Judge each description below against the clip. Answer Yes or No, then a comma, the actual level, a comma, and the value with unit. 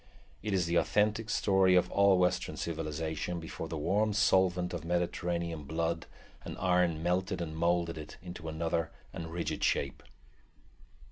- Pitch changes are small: Yes, narrow, 2.2 semitones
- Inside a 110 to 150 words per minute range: Yes, average, 145 wpm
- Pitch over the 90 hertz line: No, very low, 85 Hz